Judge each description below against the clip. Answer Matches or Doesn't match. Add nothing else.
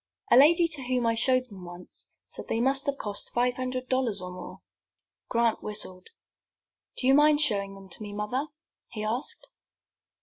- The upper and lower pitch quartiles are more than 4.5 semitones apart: Doesn't match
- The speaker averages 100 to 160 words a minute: Doesn't match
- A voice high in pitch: Matches